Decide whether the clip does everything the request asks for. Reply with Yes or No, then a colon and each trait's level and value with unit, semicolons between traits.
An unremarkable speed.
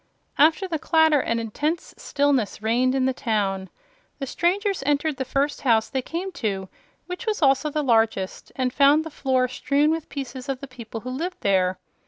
Yes: average, 185 wpm